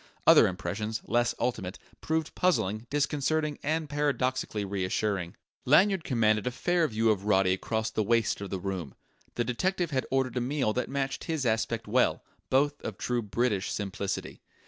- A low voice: Yes, low, 120 Hz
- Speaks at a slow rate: No, average, 160 wpm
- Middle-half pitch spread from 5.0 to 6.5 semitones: Yes, wide, 5.6 semitones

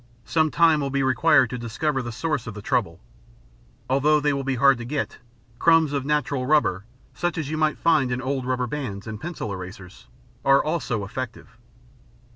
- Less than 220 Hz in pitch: Yes, low, 135 Hz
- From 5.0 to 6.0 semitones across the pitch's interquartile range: No, average, 4.1 semitones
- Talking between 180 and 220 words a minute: Yes, average, 185 wpm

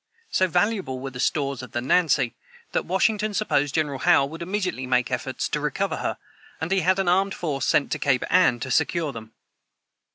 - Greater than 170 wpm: Yes, average, 195 wpm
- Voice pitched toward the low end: No, medium, 155 Hz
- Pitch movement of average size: No, wide, 5.9 semitones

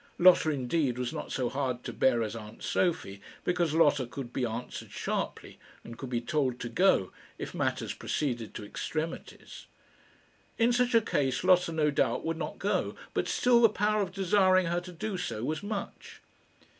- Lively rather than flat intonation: Yes, wide, 6.9 semitones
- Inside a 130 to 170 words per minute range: No, average, 180 wpm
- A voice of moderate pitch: Yes, medium, 155 Hz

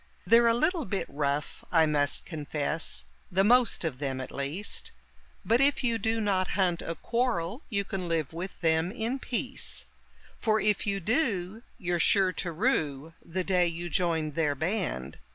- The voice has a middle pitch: Yes, medium, 180 Hz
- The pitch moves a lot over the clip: Yes, wide, 5.8 semitones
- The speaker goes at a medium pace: Yes, average, 170 wpm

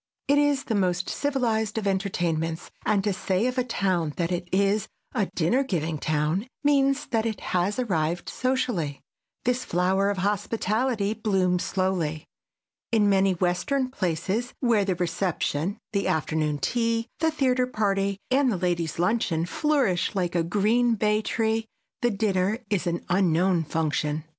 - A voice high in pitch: Yes, high, 195 Hz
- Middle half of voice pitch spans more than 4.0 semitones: Yes, average, 4.7 semitones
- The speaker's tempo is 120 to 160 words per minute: Yes, average, 150 wpm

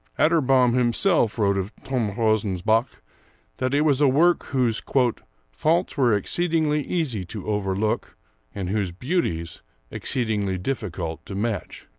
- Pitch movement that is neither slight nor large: No, wide, 6.1 semitones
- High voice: No, low, 115 Hz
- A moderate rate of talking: No, slow, 125 wpm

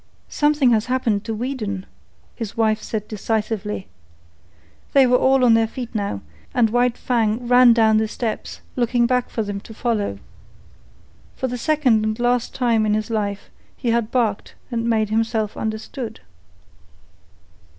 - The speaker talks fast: No, average, 150 wpm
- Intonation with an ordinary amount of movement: No, narrow, 2.3 semitones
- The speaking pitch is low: No, high, 225 Hz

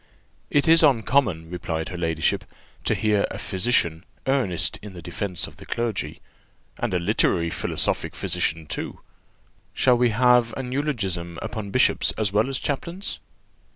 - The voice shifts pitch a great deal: Yes, wide, 6.4 semitones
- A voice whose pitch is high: No, low, 105 Hz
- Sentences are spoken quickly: No, average, 150 wpm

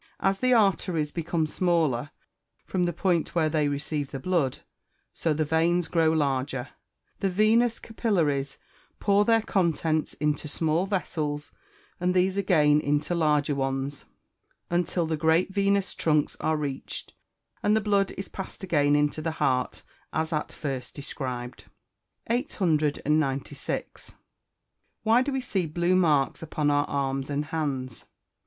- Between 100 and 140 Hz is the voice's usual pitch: No, medium, 160 Hz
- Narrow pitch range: No, average, 4.1 semitones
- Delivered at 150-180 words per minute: No, average, 140 wpm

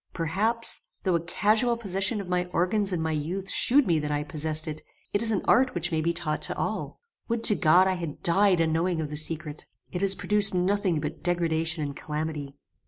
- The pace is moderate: No, fast, 210 wpm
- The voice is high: No, medium, 175 Hz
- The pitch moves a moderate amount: Yes, average, 3.9 semitones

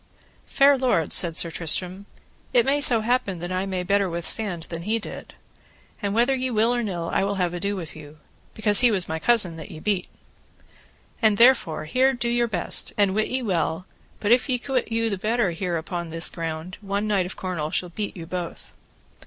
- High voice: Yes, high, 195 Hz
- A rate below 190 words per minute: No, fast, 205 wpm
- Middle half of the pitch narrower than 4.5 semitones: No, average, 5.1 semitones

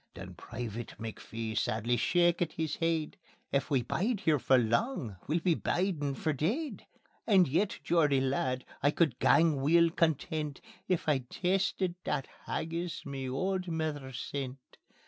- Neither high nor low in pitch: Yes, medium, 150 Hz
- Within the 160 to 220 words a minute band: No, average, 145 wpm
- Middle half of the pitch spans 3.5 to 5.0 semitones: Yes, average, 4.7 semitones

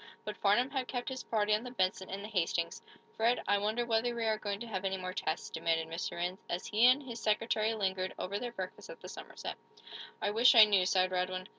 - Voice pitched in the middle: No, high, 210 Hz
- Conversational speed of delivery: No, fast, 235 wpm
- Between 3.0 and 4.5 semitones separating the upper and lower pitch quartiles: Yes, average, 3.9 semitones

